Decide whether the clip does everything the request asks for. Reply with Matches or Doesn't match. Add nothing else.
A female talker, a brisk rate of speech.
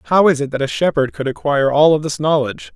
Doesn't match